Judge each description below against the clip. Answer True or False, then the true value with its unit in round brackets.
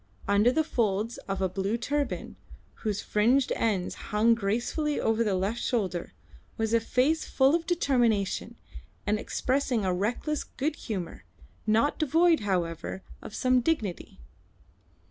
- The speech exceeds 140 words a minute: False (135 wpm)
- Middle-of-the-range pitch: False (230 Hz)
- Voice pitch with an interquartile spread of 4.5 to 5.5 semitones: True (5.2 semitones)